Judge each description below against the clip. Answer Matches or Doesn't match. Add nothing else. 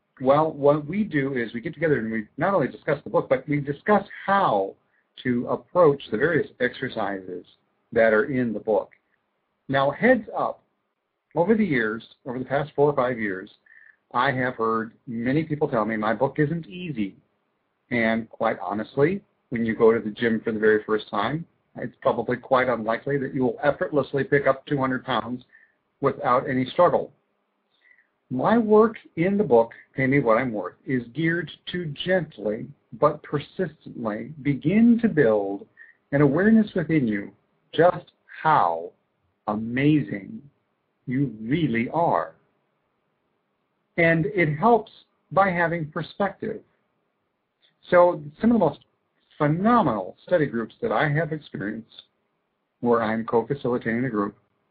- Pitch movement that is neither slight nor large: Doesn't match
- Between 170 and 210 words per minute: Doesn't match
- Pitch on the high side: Doesn't match